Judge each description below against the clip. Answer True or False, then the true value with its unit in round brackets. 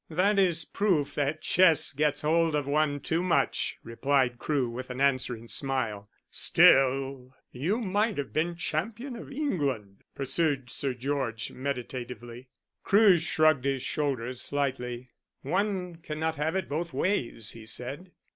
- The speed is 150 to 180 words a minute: False (135 wpm)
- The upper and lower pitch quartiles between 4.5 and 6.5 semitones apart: True (4.8 semitones)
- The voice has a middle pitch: True (145 Hz)